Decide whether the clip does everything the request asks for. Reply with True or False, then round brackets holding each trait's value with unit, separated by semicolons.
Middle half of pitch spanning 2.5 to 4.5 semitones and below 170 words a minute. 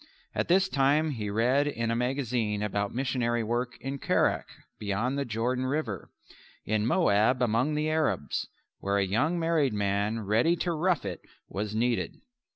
False (5.1 semitones; 160 wpm)